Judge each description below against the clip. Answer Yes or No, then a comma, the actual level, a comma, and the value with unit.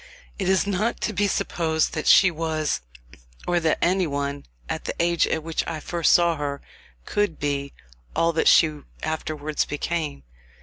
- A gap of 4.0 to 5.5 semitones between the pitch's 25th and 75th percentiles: No, narrow, 2.4 semitones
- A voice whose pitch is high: No, medium, 160 Hz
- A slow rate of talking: No, average, 165 wpm